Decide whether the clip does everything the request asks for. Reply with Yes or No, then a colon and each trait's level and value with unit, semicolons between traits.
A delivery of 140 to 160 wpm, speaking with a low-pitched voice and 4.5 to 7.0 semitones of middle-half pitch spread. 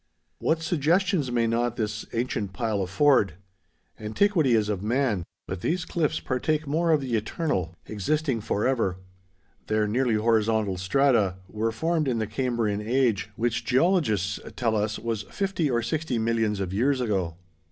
Yes: average, 145 wpm; low, 115 Hz; average, 4.9 semitones